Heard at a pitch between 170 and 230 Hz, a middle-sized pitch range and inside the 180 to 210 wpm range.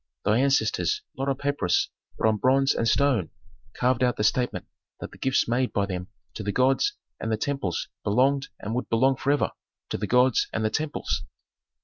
No: low, 125 Hz; average, 3.9 semitones; average, 190 wpm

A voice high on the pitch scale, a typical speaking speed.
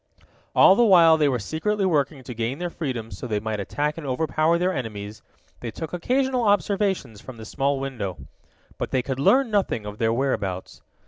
No: medium, 140 Hz; average, 190 wpm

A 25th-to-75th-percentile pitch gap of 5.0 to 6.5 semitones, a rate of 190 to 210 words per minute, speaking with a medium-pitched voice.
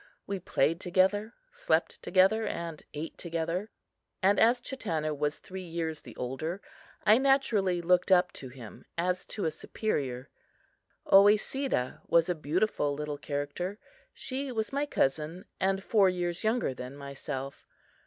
No: wide, 5.6 semitones; average, 140 wpm; medium, 180 Hz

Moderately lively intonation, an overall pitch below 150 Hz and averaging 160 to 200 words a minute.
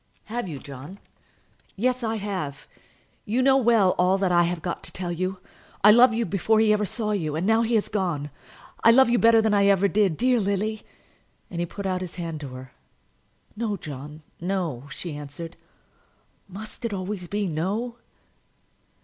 No: average, 4.5 semitones; high, 195 Hz; average, 185 wpm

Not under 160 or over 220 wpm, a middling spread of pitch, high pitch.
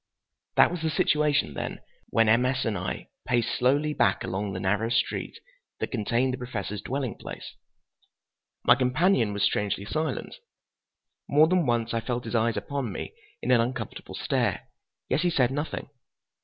No: average, 165 wpm; average, 4.3 semitones; low, 125 Hz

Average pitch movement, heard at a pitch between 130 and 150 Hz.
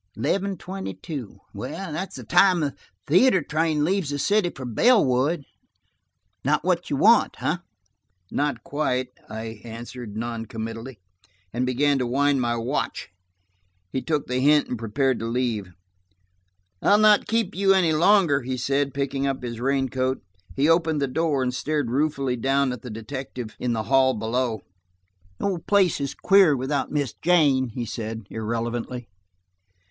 Yes: average, 4.5 semitones; low, 135 Hz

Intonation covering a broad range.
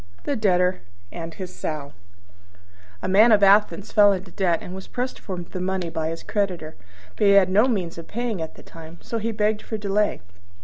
No: average, 3.4 semitones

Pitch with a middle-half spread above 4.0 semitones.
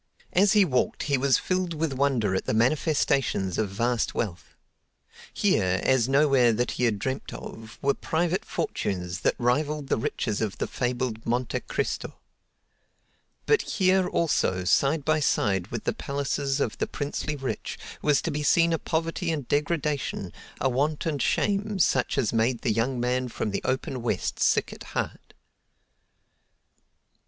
Yes: average, 4.8 semitones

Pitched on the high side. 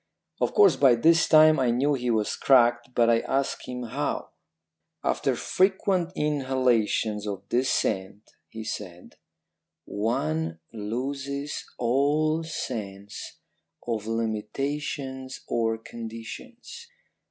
No: low, 125 Hz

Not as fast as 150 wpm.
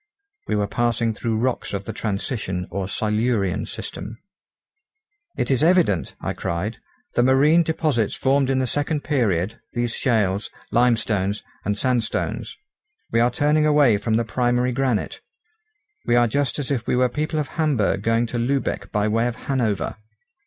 No: average, 160 wpm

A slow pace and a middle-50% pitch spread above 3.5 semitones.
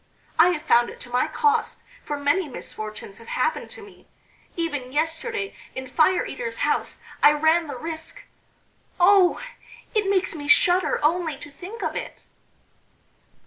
No: average, 150 wpm; average, 4.7 semitones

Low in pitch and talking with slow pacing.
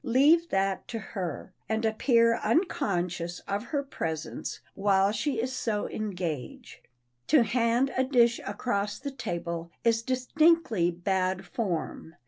No: high, 220 Hz; slow, 125 wpm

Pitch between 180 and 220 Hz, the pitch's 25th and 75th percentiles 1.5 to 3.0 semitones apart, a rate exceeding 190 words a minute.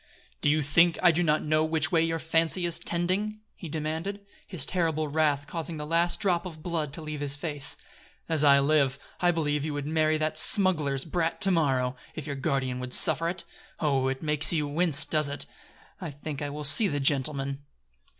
No: medium, 155 Hz; narrow, 2.6 semitones; average, 200 wpm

